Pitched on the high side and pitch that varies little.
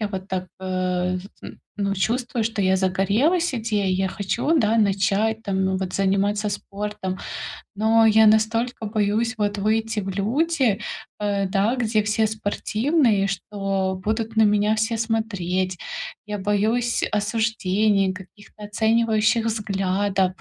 Yes: high, 210 Hz; narrow, 2.3 semitones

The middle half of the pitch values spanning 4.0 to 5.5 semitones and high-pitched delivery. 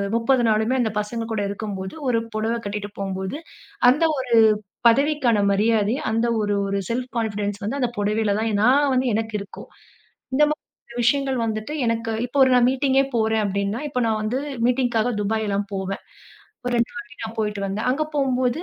No: average, 3.3 semitones; high, 225 Hz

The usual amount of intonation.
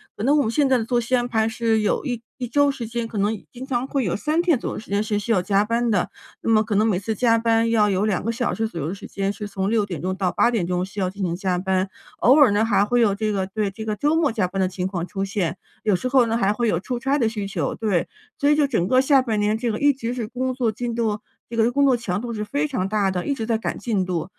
Yes: average, 3.5 semitones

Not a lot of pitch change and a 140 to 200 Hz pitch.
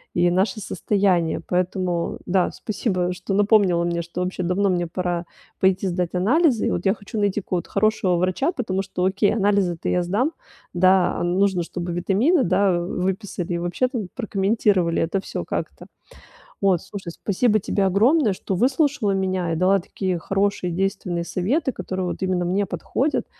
Yes: narrow, 2.3 semitones; high, 190 Hz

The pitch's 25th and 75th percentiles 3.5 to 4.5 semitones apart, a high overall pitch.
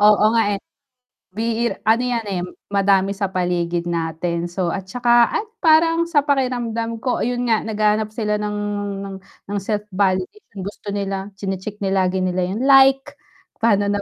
Yes: average, 3.8 semitones; high, 210 Hz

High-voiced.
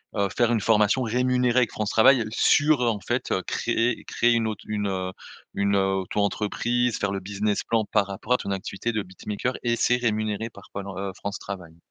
No: low, 110 Hz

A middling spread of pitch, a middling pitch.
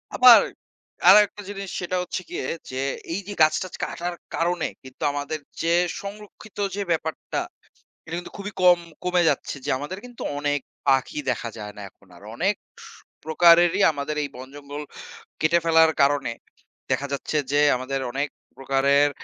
Yes: average, 4.2 semitones; medium, 160 Hz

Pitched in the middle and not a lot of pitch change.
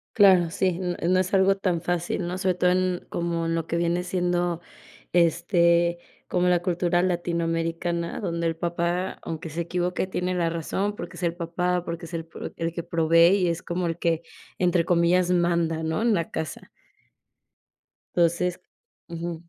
Yes: medium, 175 Hz; narrow, 1.2 semitones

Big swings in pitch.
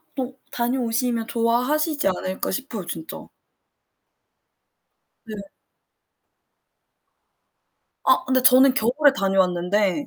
No: average, 4.9 semitones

